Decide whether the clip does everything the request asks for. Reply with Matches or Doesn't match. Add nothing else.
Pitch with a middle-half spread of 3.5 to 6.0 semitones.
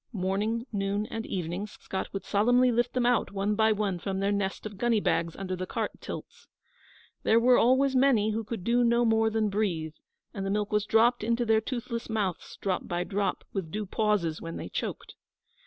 Doesn't match